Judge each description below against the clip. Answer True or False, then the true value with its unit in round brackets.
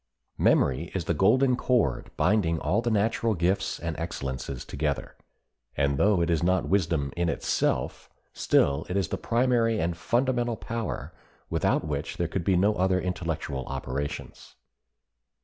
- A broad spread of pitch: True (5.7 semitones)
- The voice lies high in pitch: False (90 Hz)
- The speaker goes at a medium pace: True (150 wpm)